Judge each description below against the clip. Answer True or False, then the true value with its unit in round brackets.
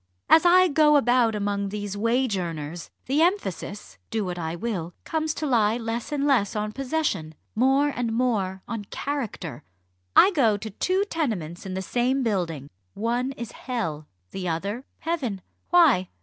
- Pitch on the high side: True (225 Hz)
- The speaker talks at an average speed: True (160 wpm)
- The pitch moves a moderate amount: False (6.2 semitones)